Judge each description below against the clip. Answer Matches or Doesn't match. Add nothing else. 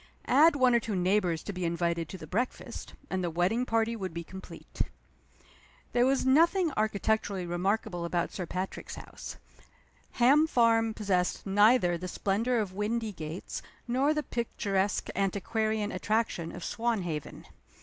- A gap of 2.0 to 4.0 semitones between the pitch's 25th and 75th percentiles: Doesn't match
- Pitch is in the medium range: Doesn't match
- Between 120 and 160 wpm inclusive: Matches